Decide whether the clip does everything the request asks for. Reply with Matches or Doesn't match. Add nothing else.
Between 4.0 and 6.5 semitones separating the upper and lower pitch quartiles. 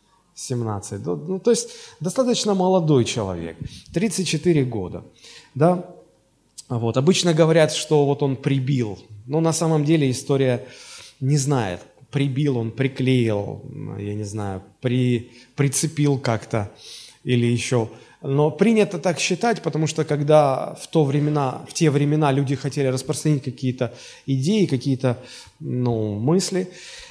Matches